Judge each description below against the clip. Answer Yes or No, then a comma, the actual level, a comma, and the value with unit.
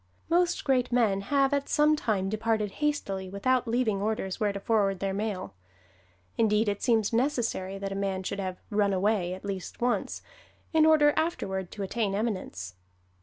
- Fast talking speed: No, average, 170 wpm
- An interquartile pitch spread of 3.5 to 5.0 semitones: Yes, average, 4.1 semitones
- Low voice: No, high, 210 Hz